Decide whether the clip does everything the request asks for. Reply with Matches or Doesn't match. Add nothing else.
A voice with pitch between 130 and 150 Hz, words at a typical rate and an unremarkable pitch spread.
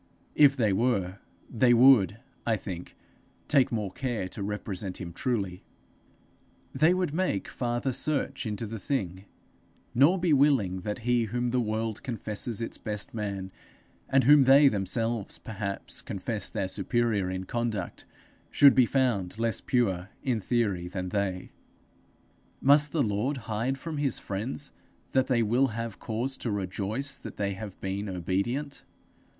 Doesn't match